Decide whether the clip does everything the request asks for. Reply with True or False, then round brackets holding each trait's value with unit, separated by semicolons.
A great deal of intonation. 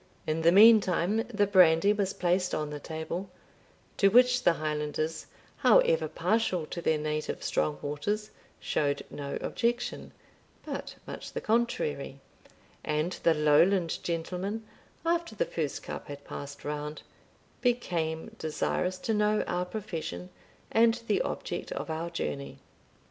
True (5.8 semitones)